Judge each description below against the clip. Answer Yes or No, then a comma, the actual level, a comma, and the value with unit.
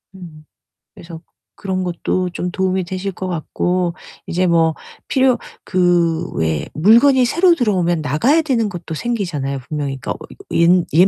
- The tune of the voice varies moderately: Yes, average, 3.8 semitones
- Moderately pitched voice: Yes, medium, 180 Hz